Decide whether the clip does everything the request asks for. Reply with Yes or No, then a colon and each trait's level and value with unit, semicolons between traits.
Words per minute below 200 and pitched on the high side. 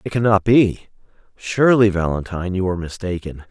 No: slow, 135 wpm; very low, 95 Hz